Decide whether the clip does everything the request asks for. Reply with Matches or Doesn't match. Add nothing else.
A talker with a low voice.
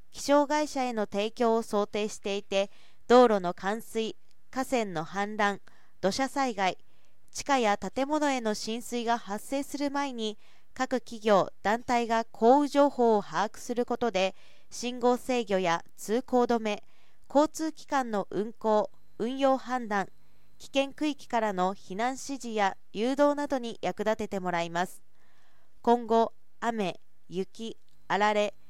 Doesn't match